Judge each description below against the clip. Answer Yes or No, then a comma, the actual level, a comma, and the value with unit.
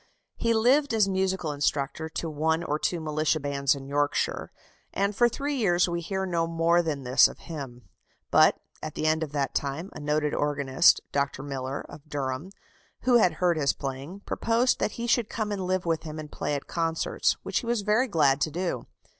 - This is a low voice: No, medium, 160 Hz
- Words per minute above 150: Yes, average, 200 wpm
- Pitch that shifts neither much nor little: Yes, average, 4.9 semitones